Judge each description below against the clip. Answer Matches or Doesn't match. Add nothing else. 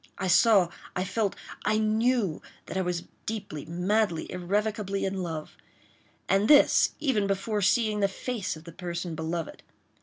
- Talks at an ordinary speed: Doesn't match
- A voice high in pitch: Matches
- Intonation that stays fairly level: Doesn't match